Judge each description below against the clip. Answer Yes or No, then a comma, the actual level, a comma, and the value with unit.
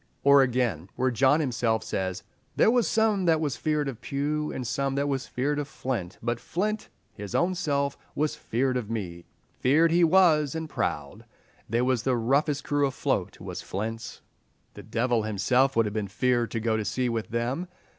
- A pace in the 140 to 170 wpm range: No, average, 185 wpm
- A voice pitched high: No, low, 130 Hz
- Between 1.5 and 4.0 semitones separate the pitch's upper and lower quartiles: No, average, 4.5 semitones